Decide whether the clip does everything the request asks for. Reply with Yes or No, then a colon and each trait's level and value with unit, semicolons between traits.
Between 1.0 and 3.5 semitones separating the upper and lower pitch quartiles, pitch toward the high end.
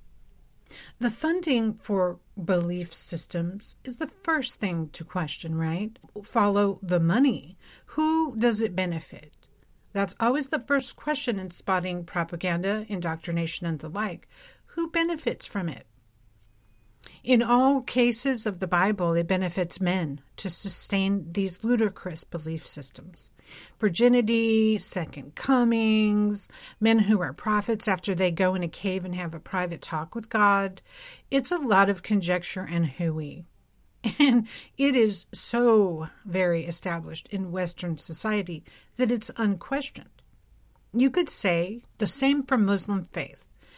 No: average, 5.2 semitones; high, 195 Hz